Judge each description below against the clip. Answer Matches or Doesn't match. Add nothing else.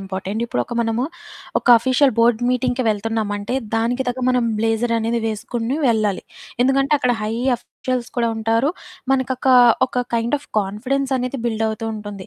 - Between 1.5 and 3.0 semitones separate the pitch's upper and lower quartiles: Matches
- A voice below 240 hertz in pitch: Matches